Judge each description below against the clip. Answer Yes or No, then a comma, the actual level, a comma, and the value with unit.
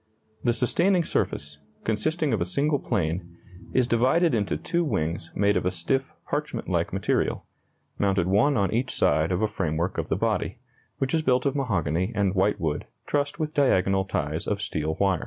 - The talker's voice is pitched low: Yes, low, 100 Hz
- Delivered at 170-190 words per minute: Yes, average, 175 wpm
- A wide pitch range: Yes, wide, 7.5 semitones